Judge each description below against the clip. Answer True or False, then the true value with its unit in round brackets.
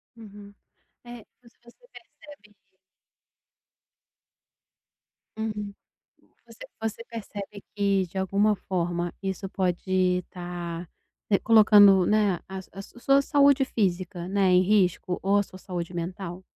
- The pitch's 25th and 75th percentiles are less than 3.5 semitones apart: True (2.8 semitones)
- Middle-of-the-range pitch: False (195 Hz)